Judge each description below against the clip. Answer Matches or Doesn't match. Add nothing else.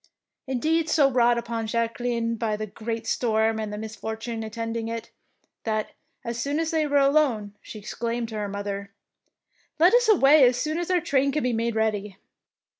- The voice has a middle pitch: Doesn't match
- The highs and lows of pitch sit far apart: Doesn't match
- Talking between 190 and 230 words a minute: Matches